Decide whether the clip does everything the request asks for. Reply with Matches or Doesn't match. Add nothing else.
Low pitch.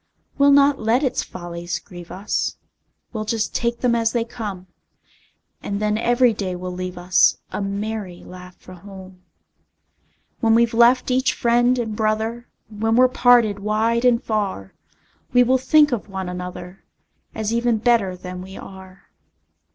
Doesn't match